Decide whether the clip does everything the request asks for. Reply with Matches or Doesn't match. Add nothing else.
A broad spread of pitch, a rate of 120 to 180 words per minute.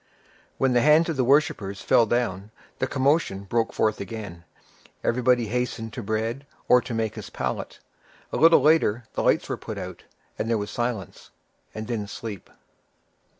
Doesn't match